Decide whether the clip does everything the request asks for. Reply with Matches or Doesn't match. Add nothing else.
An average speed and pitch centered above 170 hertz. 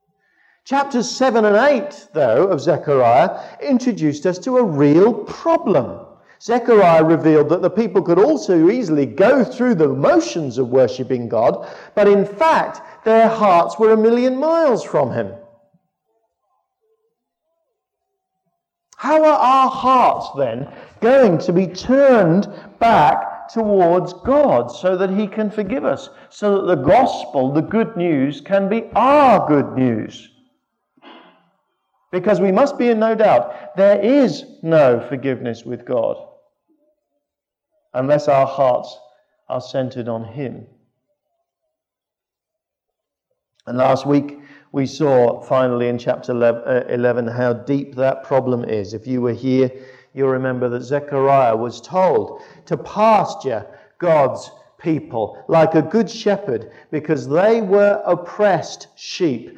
Doesn't match